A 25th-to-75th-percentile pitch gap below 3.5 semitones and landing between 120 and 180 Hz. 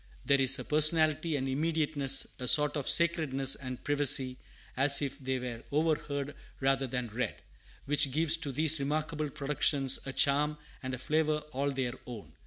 Yes: narrow, 2.4 semitones; medium, 140 Hz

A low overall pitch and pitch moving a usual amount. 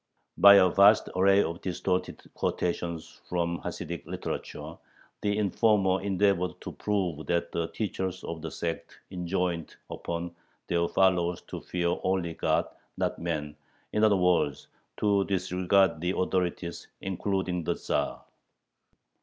No: very low, 90 Hz; narrow, 2.3 semitones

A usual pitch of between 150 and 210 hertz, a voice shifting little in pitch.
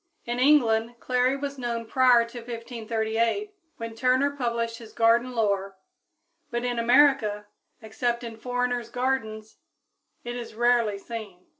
No: high, 235 Hz; narrow, 1.8 semitones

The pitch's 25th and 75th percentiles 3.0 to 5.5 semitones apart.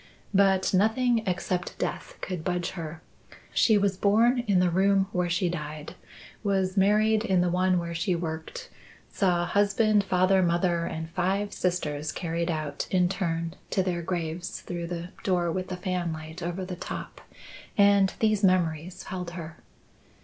No: narrow, 2.4 semitones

